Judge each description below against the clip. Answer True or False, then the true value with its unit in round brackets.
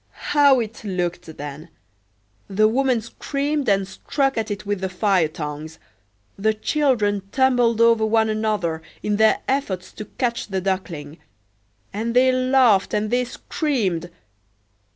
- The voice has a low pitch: False (215 Hz)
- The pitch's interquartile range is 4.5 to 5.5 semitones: True (4.8 semitones)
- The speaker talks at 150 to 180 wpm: False (135 wpm)